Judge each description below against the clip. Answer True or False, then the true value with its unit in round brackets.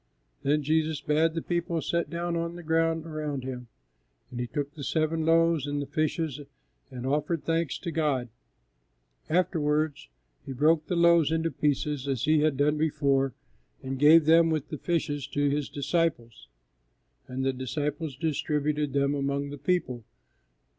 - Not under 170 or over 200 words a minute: False (160 wpm)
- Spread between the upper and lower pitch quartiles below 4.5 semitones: True (2.7 semitones)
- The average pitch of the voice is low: False (150 Hz)